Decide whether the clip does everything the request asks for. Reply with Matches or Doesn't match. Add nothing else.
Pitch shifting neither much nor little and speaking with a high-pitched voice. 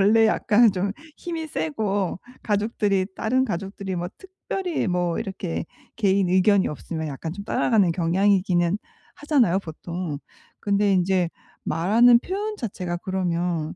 Matches